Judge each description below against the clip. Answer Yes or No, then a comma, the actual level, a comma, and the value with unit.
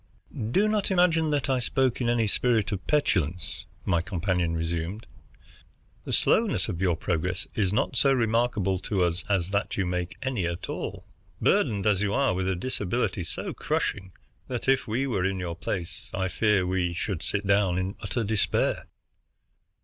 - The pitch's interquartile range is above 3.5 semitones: Yes, average, 4.8 semitones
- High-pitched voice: No, low, 100 Hz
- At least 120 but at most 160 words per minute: No, average, 170 wpm